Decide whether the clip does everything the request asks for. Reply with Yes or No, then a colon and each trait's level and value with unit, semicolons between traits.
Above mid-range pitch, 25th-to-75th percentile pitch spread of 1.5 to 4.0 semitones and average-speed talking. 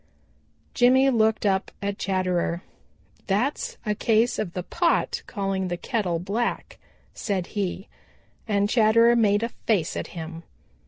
No: high, 205 Hz; average, 3.6 semitones; slow, 130 wpm